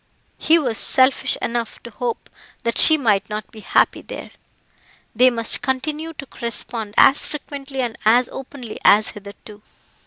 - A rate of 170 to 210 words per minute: No, average, 150 wpm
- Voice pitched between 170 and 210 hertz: No, high, 240 Hz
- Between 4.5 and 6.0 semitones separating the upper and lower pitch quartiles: No, average, 3.8 semitones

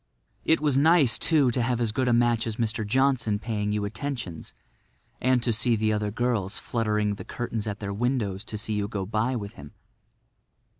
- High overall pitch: No, low, 115 Hz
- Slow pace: No, average, 195 wpm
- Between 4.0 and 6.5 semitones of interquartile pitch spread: No, average, 2.9 semitones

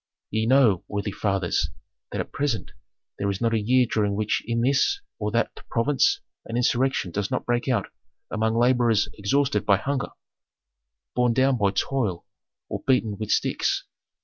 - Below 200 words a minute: Yes, average, 160 wpm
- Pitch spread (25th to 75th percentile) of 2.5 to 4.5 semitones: Yes, average, 3.9 semitones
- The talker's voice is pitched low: Yes, low, 115 Hz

